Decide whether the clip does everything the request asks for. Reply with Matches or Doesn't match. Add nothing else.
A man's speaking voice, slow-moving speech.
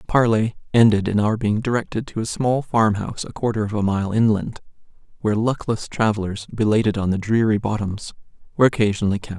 Doesn't match